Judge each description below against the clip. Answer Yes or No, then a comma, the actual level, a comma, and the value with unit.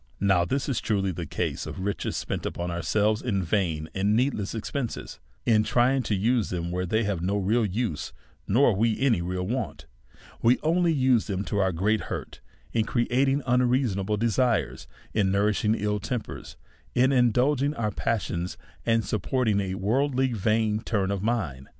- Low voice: Yes, low, 110 Hz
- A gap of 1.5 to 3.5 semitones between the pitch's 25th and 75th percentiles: No, average, 4.2 semitones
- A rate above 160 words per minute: Yes, average, 170 wpm